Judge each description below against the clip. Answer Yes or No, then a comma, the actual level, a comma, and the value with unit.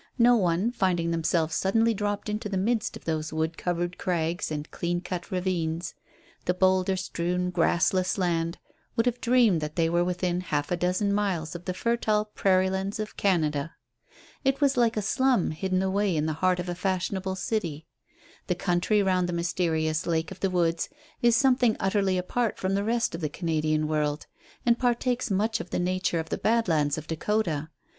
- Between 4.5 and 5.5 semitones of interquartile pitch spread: No, average, 3.9 semitones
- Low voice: No, medium, 185 Hz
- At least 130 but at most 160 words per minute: No, average, 185 wpm